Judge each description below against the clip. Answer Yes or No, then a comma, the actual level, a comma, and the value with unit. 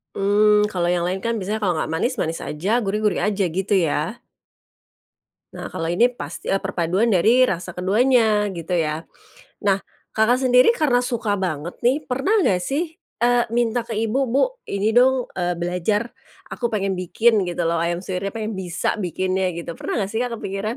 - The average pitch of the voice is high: Yes, high, 205 Hz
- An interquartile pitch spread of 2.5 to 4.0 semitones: No, average, 4.8 semitones